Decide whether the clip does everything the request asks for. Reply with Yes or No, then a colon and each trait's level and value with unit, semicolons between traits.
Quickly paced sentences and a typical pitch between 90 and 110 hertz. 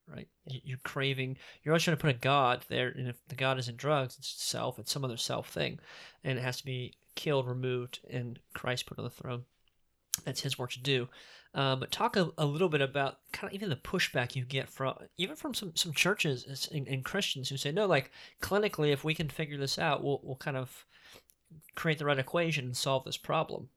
No: fast, 225 wpm; low, 135 Hz